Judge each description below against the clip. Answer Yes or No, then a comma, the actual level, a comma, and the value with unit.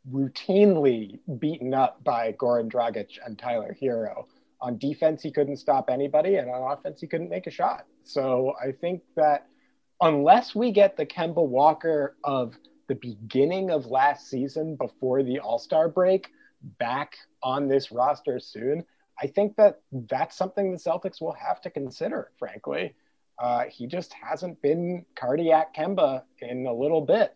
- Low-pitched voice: No, medium, 150 Hz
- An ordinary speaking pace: Yes, average, 160 wpm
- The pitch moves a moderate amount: Yes, average, 5.0 semitones